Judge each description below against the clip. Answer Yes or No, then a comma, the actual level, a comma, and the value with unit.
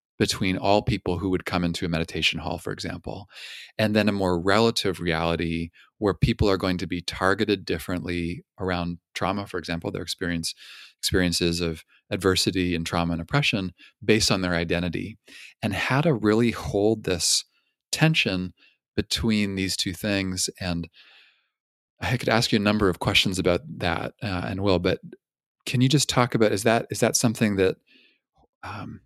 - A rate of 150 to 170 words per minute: Yes, average, 165 wpm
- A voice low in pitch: Yes, very low, 95 Hz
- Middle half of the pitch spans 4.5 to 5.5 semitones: No, average, 3.7 semitones